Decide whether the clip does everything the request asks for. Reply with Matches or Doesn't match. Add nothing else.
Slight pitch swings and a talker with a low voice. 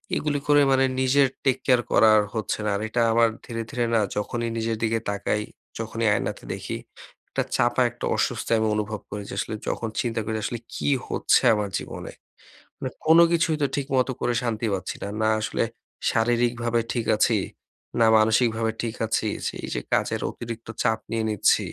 Matches